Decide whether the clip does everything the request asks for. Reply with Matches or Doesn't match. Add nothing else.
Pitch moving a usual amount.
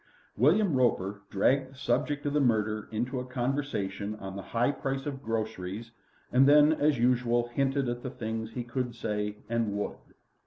Matches